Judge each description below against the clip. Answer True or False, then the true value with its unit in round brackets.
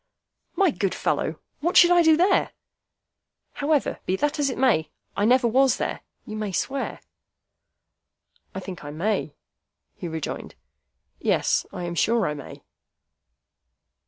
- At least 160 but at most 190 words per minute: False (140 wpm)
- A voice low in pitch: False (230 Hz)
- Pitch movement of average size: False (8.4 semitones)